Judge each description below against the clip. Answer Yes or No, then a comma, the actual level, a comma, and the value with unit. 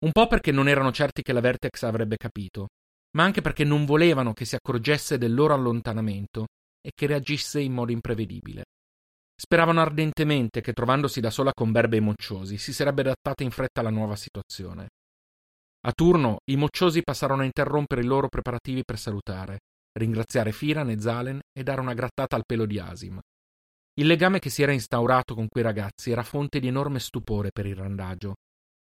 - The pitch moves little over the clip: No, average, 5.0 semitones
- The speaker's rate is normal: No, fast, 180 wpm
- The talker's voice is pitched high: No, low, 125 Hz